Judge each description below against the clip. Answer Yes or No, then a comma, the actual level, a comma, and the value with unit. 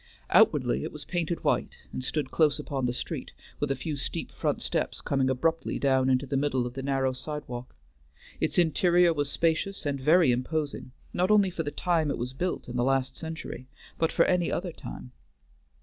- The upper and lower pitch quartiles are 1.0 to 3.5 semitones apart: No, average, 4.0 semitones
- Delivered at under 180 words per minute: No, average, 195 wpm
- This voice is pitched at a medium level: Yes, medium, 145 Hz